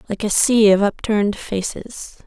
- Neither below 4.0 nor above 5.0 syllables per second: Yes, 4.5 syllables/s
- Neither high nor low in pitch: No, high, 210 Hz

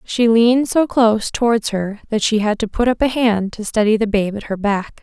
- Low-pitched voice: No, high, 220 Hz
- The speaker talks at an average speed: No, fast, 250 wpm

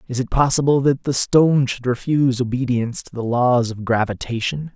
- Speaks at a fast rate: No, average, 175 wpm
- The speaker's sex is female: No, male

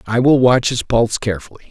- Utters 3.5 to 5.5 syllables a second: No, 6.5 syllables/s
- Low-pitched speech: Yes, low, 120 Hz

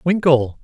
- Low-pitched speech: No, medium, 150 Hz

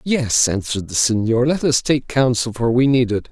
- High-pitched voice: No, low, 120 Hz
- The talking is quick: Yes, fast, 215 wpm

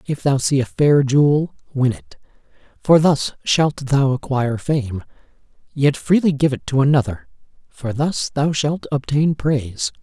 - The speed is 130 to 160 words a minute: Yes, average, 155 wpm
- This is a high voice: No, medium, 140 Hz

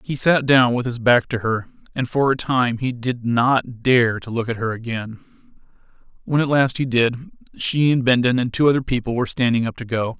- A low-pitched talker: Yes, low, 125 Hz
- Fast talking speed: Yes, fast, 225 wpm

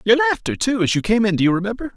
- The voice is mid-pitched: No, high, 195 Hz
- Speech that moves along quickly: Yes, fast, 305 wpm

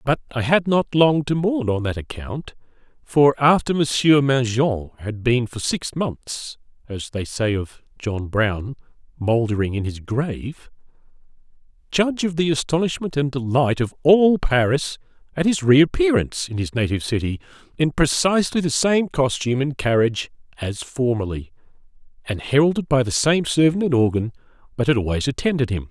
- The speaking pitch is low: Yes, low, 130 Hz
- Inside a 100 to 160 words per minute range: Yes, average, 150 wpm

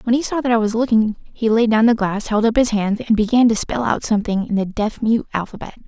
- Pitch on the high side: Yes, high, 225 Hz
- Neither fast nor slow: No, fast, 275 wpm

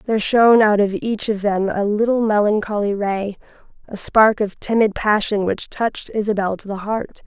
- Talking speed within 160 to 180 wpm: Yes, average, 175 wpm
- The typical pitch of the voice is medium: No, high, 210 Hz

